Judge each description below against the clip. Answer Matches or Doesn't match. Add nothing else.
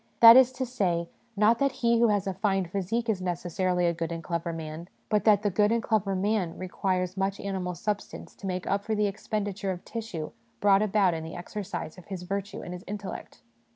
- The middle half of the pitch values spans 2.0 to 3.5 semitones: Matches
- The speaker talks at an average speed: Doesn't match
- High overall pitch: Matches